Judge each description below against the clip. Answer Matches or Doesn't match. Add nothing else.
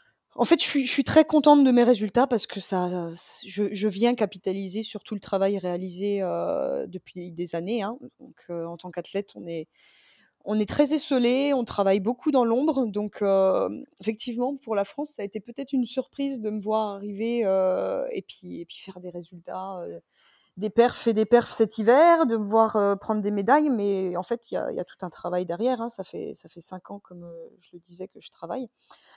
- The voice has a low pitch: Doesn't match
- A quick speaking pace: Matches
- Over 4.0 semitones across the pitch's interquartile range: Matches